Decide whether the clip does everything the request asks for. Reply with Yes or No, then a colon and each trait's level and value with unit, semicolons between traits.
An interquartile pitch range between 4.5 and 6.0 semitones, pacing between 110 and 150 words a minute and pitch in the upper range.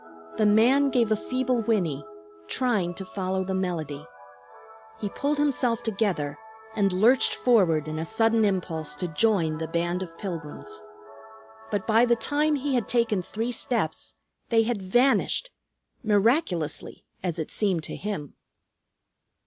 Yes: wide, 5.5 semitones; average, 140 wpm; high, 205 Hz